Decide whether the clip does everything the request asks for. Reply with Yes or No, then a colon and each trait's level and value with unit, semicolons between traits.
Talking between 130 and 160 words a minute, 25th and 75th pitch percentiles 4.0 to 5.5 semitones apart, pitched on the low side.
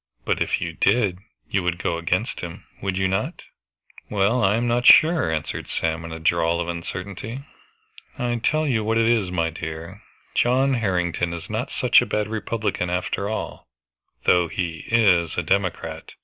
No: average, 175 wpm; average, 5.0 semitones; very low, 95 Hz